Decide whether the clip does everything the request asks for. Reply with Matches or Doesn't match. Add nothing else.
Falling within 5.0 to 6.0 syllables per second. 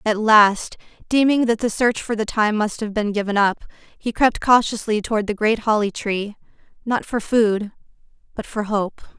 Doesn't match